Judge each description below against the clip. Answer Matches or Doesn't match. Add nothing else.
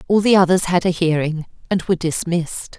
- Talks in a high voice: Doesn't match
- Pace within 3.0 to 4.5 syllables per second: Doesn't match